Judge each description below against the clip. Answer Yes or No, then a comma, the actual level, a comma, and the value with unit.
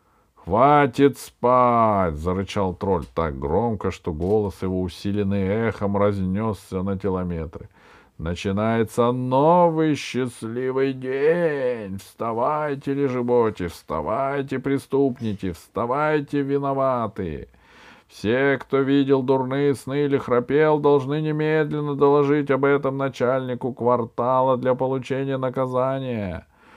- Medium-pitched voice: No, low, 130 Hz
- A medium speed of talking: No, slow, 90 wpm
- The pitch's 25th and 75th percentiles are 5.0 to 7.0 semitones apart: Yes, wide, 5.4 semitones